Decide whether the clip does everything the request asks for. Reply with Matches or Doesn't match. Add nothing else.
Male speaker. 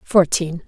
Doesn't match